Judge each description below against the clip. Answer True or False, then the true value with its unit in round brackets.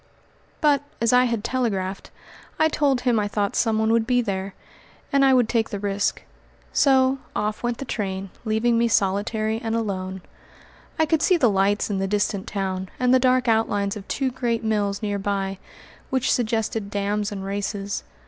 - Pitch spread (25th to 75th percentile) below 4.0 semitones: True (3.6 semitones)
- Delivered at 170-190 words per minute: True (175 wpm)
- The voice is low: False (220 Hz)